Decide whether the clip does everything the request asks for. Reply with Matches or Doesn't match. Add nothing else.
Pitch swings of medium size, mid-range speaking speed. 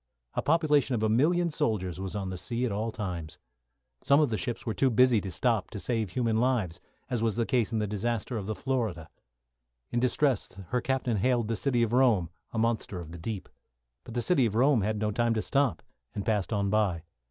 Doesn't match